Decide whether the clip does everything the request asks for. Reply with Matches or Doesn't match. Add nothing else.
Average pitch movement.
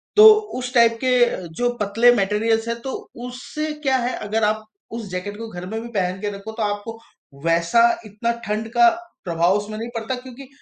Matches